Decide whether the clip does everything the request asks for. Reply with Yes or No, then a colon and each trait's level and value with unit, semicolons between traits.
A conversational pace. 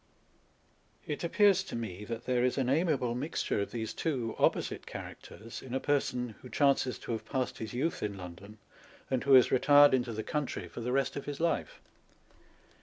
Yes: average, 185 wpm